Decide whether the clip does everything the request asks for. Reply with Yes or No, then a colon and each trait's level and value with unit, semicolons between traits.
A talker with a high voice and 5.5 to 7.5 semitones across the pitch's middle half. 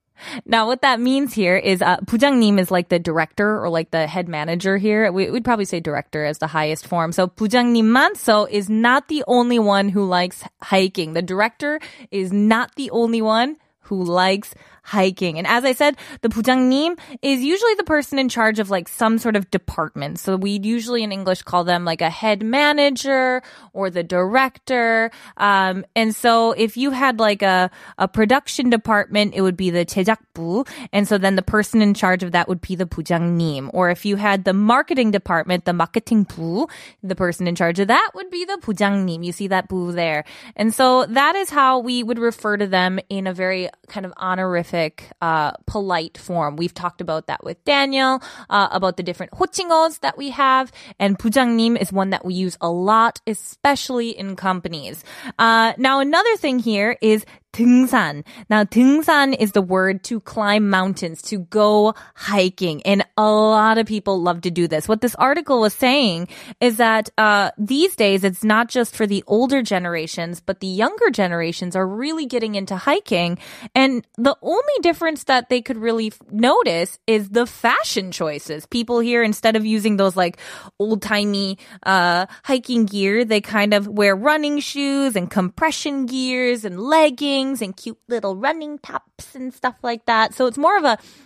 No: high, 215 Hz; average, 5.1 semitones